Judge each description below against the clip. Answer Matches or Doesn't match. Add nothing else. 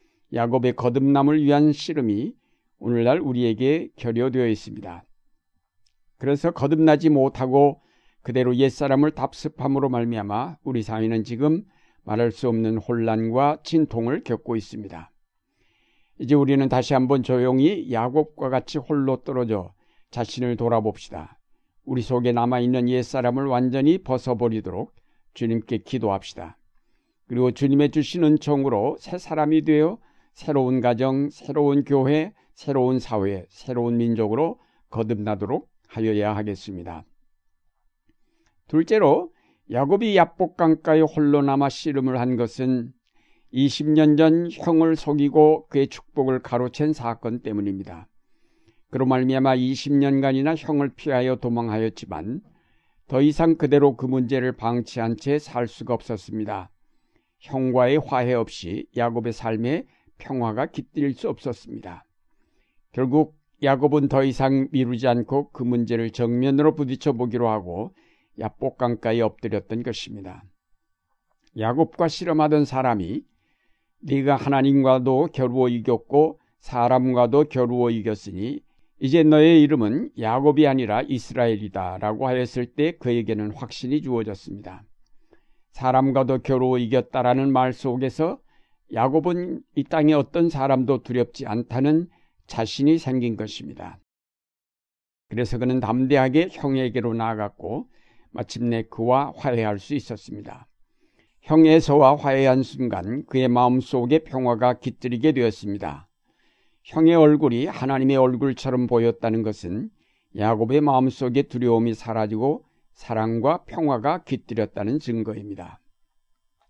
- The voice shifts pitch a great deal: Doesn't match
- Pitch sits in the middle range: Doesn't match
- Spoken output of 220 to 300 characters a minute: Matches